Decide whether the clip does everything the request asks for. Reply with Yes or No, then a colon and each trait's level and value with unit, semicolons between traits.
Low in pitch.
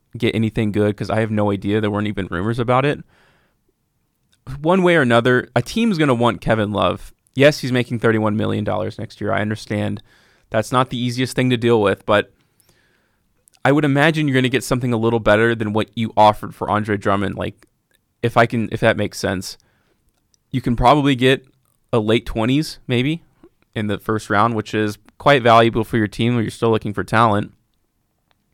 Yes: low, 115 Hz